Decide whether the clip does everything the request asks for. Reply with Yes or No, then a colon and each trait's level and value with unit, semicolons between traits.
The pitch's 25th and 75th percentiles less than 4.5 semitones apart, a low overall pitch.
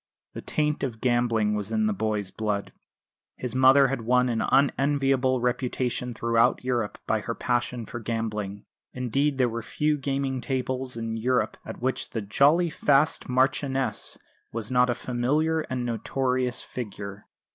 Yes: average, 2.8 semitones; low, 125 Hz